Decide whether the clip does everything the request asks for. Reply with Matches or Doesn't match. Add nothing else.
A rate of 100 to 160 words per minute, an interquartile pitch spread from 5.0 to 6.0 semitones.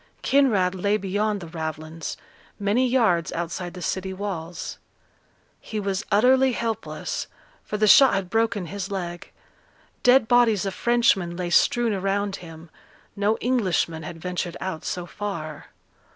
Doesn't match